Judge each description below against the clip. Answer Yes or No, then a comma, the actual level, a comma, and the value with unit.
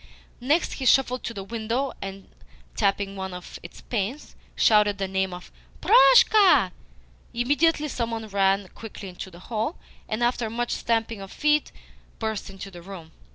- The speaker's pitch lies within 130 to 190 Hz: No, high, 220 Hz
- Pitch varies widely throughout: No, average, 4.2 semitones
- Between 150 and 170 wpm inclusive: Yes, average, 155 wpm